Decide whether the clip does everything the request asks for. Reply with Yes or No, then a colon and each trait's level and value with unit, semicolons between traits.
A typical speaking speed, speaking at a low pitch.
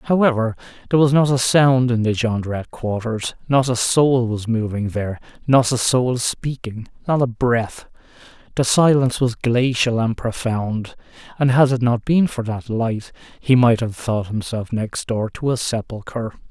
Yes: average, 170 wpm; low, 120 Hz